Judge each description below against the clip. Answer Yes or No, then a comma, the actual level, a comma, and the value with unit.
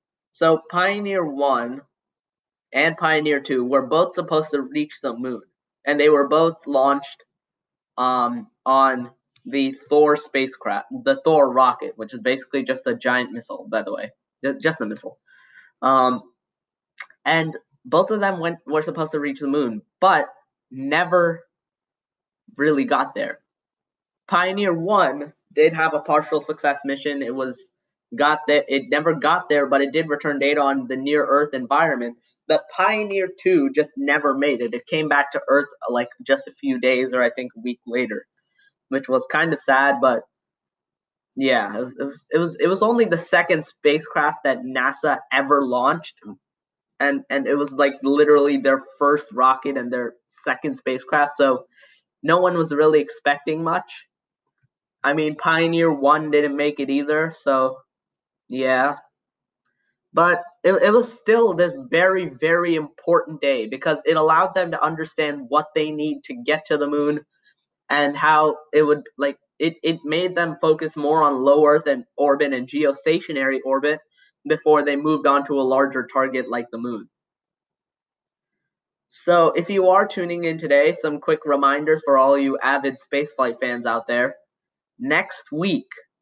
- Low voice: No, medium, 150 Hz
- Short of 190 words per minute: Yes, average, 160 wpm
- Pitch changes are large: No, average, 2.9 semitones